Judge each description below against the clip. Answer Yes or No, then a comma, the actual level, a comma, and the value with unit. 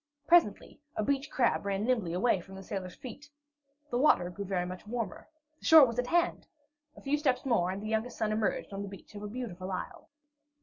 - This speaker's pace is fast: Yes, fast, 220 wpm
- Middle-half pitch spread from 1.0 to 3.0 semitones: No, average, 4.7 semitones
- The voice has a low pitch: No, high, 215 Hz